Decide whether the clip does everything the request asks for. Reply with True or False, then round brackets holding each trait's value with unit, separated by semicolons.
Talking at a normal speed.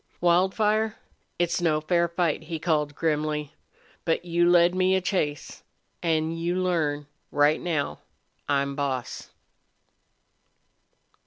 False (110 wpm)